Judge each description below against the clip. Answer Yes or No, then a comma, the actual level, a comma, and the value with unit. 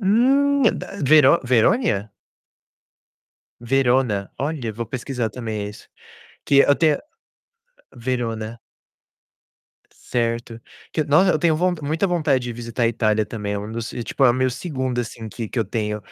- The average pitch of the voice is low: Yes, low, 125 Hz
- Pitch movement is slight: No, average, 4.7 semitones